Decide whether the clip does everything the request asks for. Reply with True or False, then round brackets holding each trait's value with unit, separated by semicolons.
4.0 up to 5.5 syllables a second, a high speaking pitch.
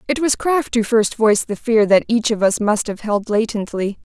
True (5.0 syllables/s; 220 Hz)